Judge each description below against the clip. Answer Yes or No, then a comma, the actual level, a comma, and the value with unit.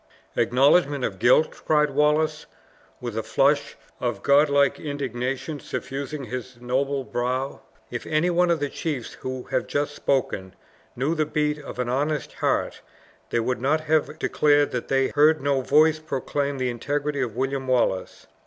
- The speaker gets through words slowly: No, average, 160 wpm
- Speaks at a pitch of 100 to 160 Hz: Yes, medium, 140 Hz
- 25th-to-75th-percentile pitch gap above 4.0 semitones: No, average, 2.7 semitones